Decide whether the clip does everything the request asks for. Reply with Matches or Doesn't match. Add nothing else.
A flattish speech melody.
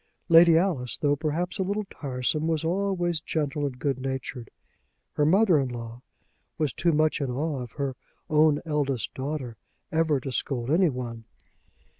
Doesn't match